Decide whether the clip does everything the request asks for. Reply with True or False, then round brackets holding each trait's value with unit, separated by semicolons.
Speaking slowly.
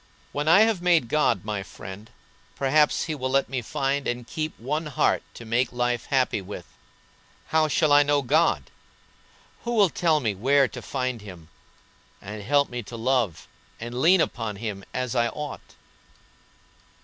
False (165 wpm)